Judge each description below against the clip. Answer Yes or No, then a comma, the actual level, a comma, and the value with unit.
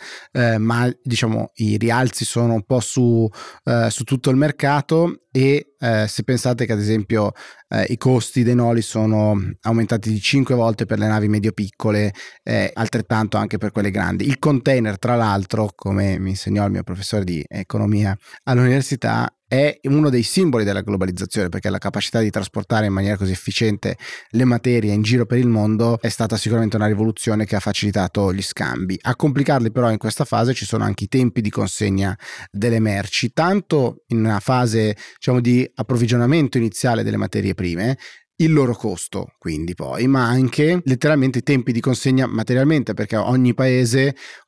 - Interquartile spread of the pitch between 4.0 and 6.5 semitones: No, average, 3.2 semitones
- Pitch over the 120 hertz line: No, low, 115 Hz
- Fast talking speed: Yes, fast, 175 wpm